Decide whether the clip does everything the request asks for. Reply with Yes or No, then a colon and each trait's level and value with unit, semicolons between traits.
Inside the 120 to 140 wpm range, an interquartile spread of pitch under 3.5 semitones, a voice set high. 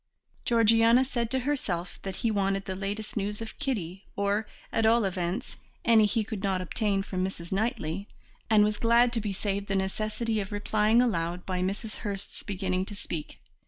No: average, 180 wpm; average, 2.9 semitones; high, 205 Hz